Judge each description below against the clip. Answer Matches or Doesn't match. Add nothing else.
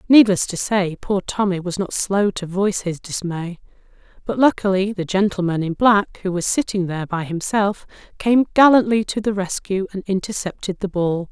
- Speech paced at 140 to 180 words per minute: Matches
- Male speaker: Doesn't match